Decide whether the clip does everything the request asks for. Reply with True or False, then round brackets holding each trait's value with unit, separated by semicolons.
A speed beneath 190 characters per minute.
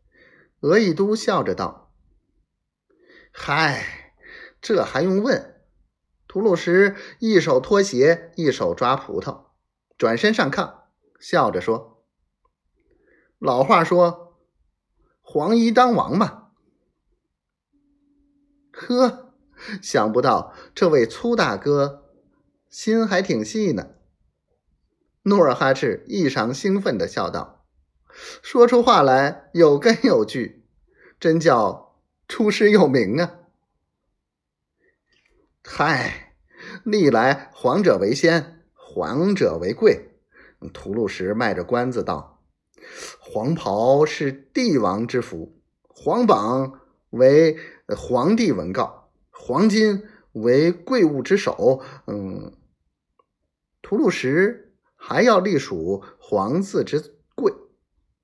True (135 characters per minute)